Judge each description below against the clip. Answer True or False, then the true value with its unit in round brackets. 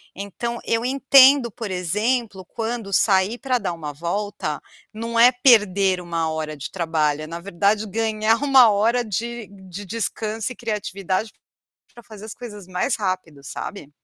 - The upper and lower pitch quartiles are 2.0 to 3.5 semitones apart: False (4.2 semitones)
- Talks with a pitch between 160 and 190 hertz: False (210 Hz)